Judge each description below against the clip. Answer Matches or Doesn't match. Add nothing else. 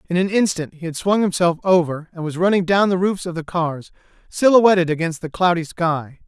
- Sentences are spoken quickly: Matches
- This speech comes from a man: Matches